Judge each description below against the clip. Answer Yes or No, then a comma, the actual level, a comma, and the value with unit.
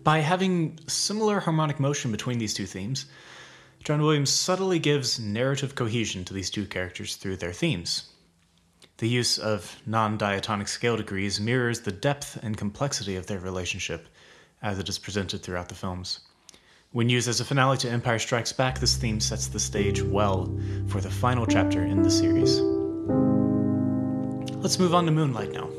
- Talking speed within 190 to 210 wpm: No, average, 170 wpm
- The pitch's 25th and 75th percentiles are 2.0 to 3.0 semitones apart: No, average, 5.3 semitones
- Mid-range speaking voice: No, low, 105 Hz